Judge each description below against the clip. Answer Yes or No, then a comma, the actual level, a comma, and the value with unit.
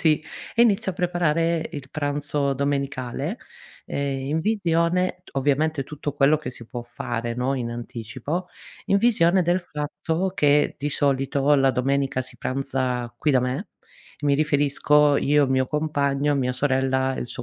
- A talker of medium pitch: Yes, medium, 145 Hz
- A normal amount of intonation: Yes, average, 3.0 semitones